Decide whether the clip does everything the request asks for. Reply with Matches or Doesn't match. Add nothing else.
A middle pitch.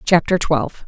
Matches